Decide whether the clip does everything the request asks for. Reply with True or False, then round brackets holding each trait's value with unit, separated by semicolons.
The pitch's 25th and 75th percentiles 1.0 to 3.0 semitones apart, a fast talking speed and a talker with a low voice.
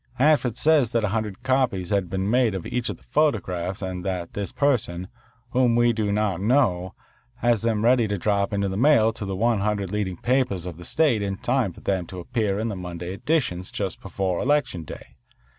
False (4.4 semitones; 210 wpm; 105 Hz)